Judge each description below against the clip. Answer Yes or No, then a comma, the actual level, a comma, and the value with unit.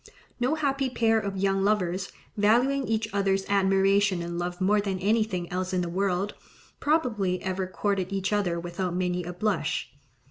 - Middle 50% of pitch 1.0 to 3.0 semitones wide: Yes, average, 2.7 semitones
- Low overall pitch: No, high, 195 Hz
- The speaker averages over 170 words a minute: No, average, 165 wpm